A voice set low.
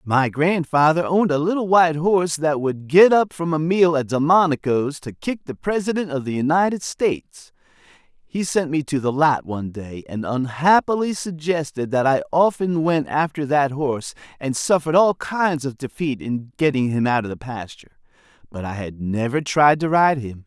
No: medium, 150 Hz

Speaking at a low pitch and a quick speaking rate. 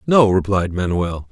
No: low, 100 Hz; slow, 135 wpm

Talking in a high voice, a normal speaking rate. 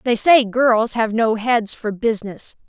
Yes: high, 225 Hz; average, 180 wpm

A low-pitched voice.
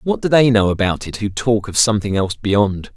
Yes: low, 110 Hz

